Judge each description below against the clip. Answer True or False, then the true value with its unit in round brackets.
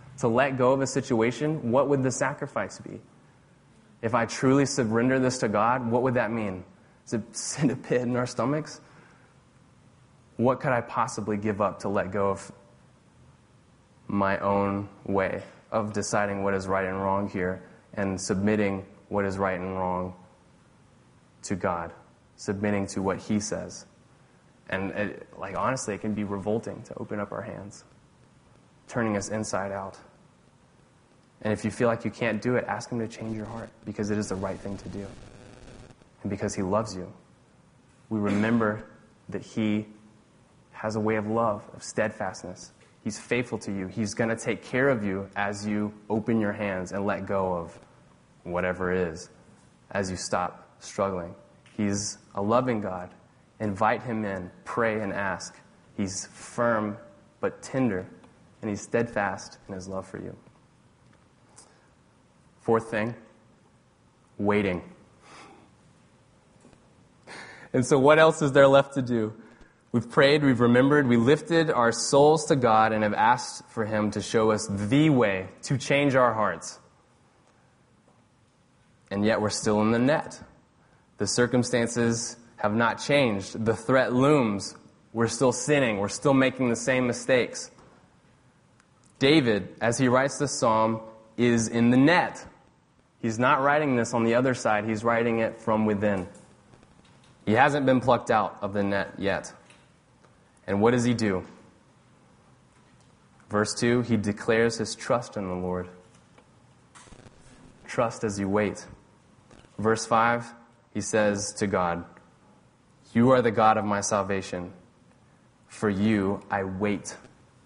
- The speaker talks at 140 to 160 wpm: True (150 wpm)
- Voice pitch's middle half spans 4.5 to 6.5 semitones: False (3.3 semitones)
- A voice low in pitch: True (110 Hz)